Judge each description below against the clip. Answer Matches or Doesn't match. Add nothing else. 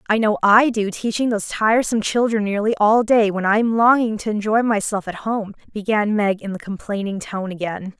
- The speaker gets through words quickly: Doesn't match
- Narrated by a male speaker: Doesn't match